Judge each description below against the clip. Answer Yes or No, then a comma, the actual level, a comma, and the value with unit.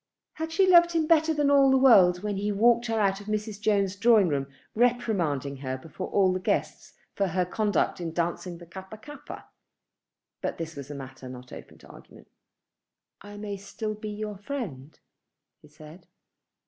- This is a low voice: No, high, 200 Hz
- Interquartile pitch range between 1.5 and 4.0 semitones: No, average, 5.2 semitones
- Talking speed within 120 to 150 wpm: No, average, 180 wpm